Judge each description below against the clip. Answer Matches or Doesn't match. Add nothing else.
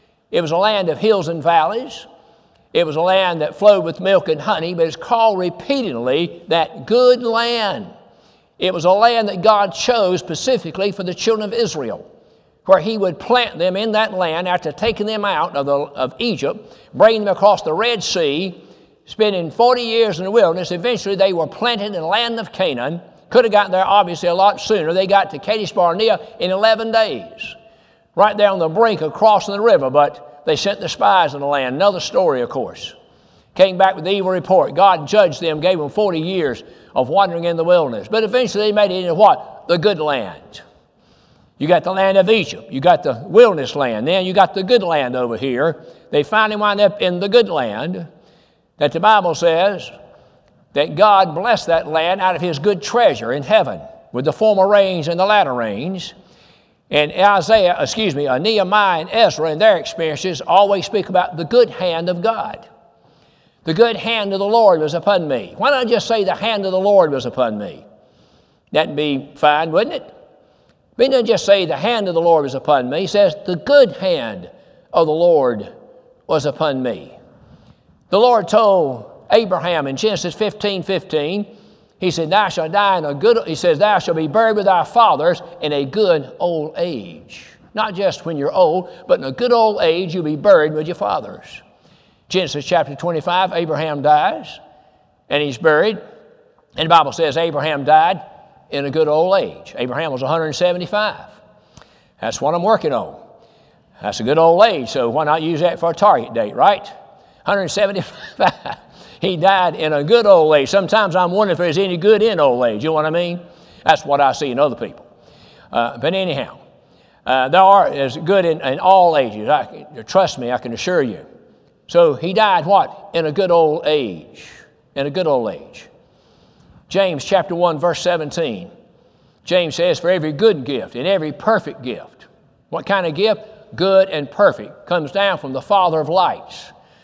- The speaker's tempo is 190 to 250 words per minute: Matches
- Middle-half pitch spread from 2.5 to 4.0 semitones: Doesn't match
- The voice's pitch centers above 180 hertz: Matches